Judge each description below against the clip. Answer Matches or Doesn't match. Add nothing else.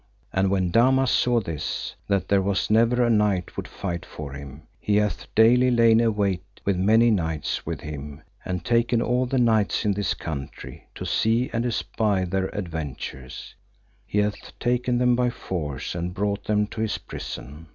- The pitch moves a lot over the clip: Doesn't match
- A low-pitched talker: Matches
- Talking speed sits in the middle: Matches